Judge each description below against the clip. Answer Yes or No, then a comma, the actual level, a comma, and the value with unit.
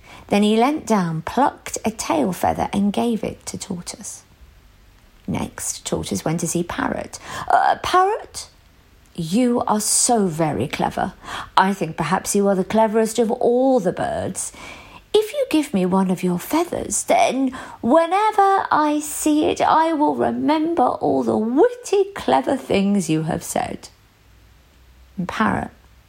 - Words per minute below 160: Yes, average, 145 wpm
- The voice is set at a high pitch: Yes, high, 220 Hz